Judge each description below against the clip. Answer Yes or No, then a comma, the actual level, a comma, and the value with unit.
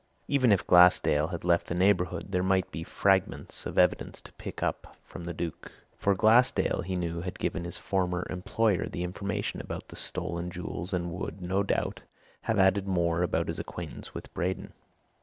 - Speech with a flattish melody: Yes, narrow, 1.9 semitones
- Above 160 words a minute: Yes, average, 180 wpm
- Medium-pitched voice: No, very low, 90 Hz